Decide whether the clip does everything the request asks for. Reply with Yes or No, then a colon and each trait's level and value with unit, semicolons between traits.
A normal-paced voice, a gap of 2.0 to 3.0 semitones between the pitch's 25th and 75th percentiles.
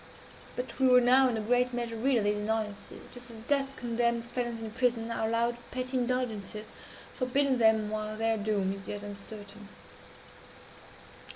Yes: average, 165 wpm; narrow, 2.5 semitones